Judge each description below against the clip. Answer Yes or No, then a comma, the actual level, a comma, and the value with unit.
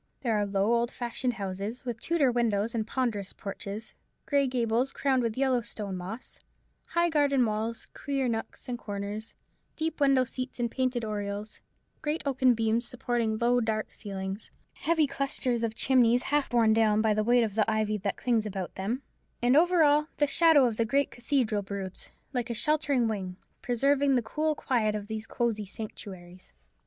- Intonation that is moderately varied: Yes, average, 3.7 semitones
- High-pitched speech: Yes, high, 235 Hz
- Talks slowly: No, average, 175 wpm